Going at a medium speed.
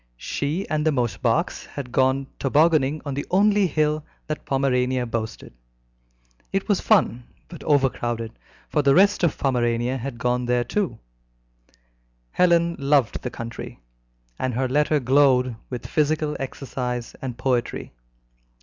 No: slow, 130 wpm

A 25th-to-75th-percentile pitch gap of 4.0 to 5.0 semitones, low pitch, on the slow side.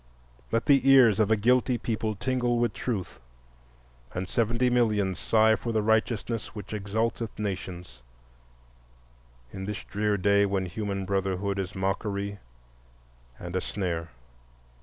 No: average, 3.0 semitones; low, 105 Hz; slow, 130 wpm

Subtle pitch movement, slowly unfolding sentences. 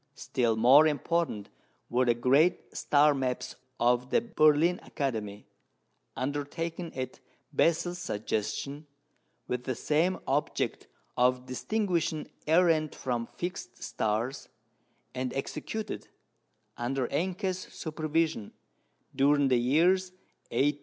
No: average, 4.8 semitones; slow, 105 wpm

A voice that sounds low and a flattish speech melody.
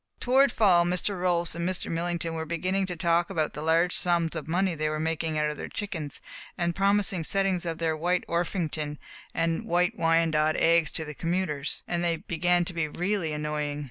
No: medium, 170 Hz; narrow, 2.1 semitones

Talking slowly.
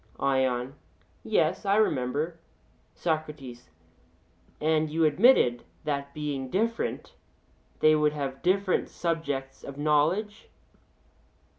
Yes: slow, 95 wpm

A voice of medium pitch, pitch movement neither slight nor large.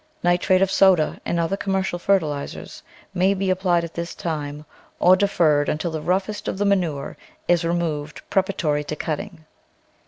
Yes: medium, 175 Hz; average, 3.6 semitones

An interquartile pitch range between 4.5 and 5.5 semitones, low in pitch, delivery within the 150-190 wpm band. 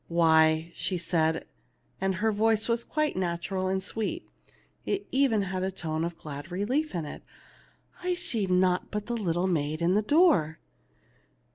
No: average, 4.8 semitones; medium, 185 Hz; average, 165 wpm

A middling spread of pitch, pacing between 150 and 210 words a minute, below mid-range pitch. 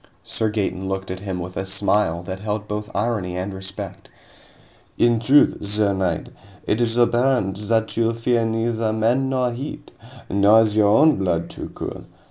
Yes: average, 3.3 semitones; average, 170 wpm; low, 105 Hz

